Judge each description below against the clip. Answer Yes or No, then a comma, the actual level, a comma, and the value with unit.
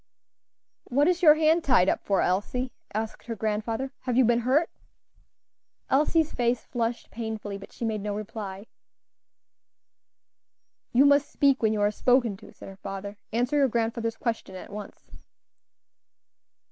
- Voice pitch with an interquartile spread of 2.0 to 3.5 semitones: No, average, 3.9 semitones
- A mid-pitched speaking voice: No, high, 230 Hz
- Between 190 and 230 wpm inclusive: No, average, 145 wpm